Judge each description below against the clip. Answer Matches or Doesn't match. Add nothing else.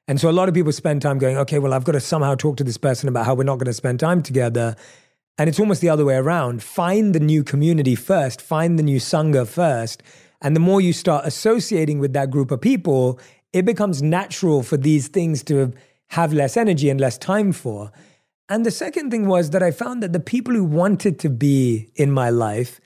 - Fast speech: Matches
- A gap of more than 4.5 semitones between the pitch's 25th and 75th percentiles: Matches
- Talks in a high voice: Doesn't match